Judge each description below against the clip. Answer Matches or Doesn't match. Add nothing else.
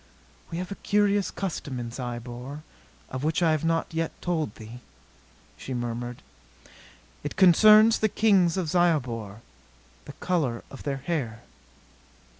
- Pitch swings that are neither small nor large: Doesn't match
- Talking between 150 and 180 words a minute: Doesn't match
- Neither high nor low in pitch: Matches